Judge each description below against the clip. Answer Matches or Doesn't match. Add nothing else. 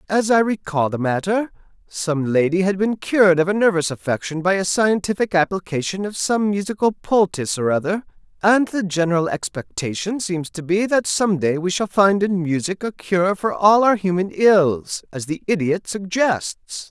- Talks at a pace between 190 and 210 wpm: Doesn't match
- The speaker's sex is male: Matches